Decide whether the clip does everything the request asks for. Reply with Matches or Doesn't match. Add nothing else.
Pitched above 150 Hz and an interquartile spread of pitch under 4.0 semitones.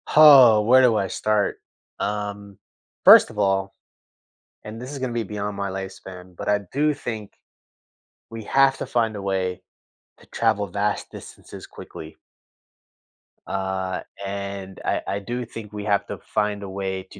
Doesn't match